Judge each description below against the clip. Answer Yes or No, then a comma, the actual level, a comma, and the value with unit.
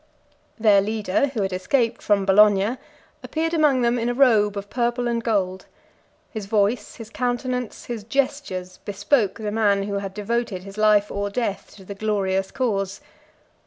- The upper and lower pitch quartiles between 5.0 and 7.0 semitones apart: No, average, 3.3 semitones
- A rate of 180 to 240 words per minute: No, average, 160 wpm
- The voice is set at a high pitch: Yes, high, 210 Hz